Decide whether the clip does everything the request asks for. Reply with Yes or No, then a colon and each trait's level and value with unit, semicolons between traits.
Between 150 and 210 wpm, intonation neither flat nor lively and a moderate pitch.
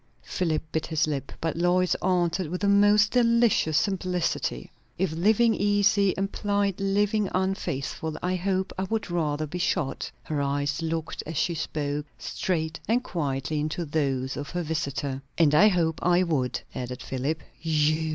Yes: average, 155 wpm; average, 4.3 semitones; medium, 170 Hz